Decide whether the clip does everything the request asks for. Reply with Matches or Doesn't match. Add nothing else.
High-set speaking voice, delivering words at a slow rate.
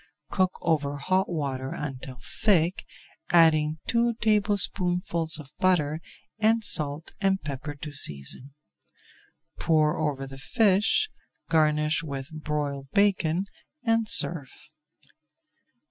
Doesn't match